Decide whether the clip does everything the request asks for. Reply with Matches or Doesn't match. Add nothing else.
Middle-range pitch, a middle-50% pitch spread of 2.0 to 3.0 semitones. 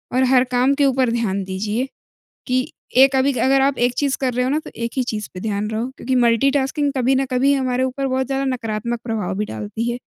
Doesn't match